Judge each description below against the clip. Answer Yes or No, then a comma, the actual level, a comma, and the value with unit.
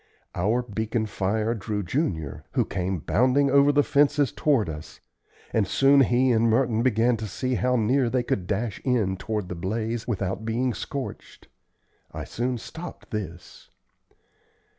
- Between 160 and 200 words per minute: No, average, 150 wpm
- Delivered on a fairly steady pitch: No, average, 4.0 semitones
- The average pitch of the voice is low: Yes, low, 115 Hz